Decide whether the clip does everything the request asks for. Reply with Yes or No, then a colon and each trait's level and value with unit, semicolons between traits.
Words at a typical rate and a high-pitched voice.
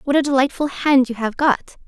No: fast, 225 wpm; very high, 265 Hz